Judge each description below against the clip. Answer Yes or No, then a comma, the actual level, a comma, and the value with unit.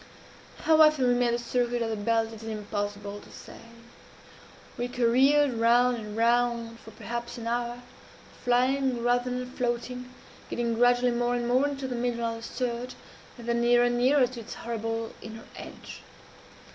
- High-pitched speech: Yes, high, 240 Hz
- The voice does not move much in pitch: Yes, narrow, 1.3 semitones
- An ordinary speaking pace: Yes, average, 170 wpm